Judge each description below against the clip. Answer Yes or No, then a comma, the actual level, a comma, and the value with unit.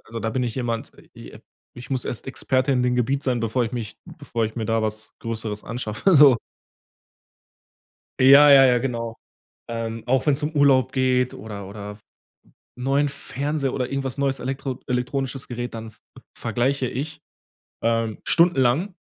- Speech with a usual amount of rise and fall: Yes, average, 3.0 semitones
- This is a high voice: No, low, 125 Hz